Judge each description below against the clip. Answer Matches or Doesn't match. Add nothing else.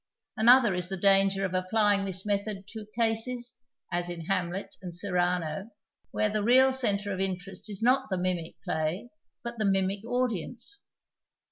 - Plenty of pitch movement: Doesn't match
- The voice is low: Doesn't match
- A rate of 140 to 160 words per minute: Matches